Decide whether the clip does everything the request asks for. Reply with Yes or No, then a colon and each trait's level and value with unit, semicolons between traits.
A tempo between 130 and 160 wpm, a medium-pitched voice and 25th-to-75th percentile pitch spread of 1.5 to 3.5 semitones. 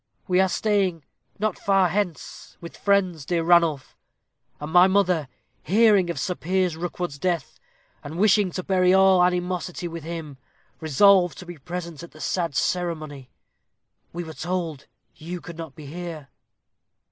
Yes: average, 150 wpm; medium, 175 Hz; narrow, 2.4 semitones